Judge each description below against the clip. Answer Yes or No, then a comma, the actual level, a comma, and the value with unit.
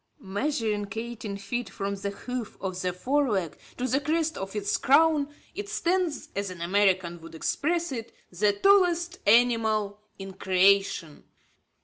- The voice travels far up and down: Yes, wide, 6.7 semitones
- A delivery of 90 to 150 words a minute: Yes, average, 145 wpm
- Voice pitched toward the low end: No, high, 215 Hz